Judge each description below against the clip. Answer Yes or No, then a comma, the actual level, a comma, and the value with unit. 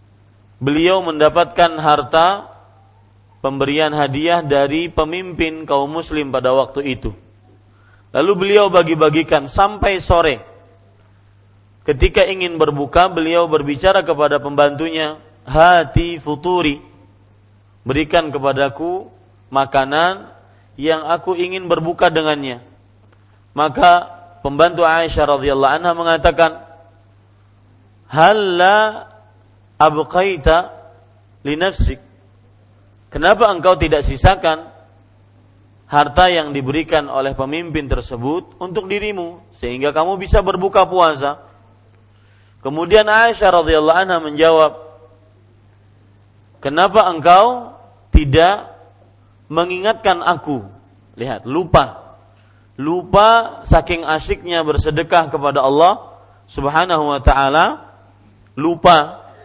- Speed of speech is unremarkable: No, slow, 80 wpm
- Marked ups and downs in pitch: Yes, wide, 8.8 semitones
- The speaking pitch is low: No, medium, 145 Hz